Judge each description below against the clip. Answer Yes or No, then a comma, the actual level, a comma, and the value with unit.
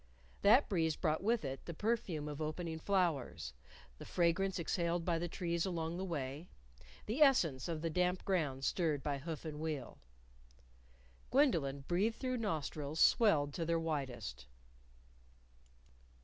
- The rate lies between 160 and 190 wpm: No, average, 140 wpm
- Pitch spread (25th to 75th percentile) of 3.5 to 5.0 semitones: Yes, average, 3.8 semitones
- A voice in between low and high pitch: Yes, medium, 165 Hz